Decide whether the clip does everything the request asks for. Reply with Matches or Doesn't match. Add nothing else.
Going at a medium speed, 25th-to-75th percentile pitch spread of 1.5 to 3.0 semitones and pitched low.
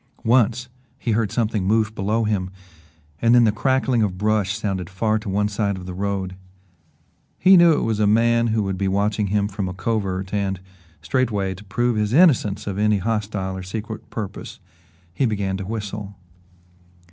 Matches